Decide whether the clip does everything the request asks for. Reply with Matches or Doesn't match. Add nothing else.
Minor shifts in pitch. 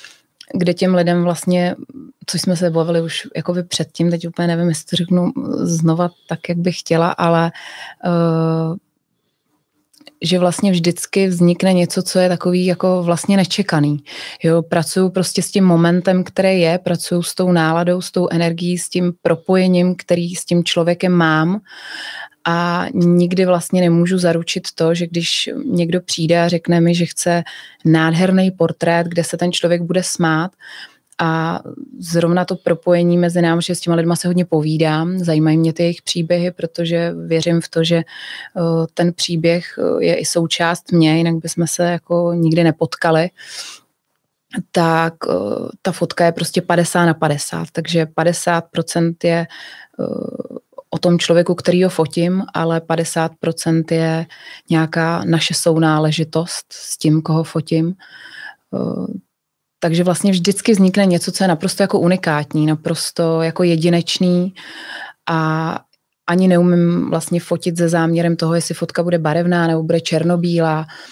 Matches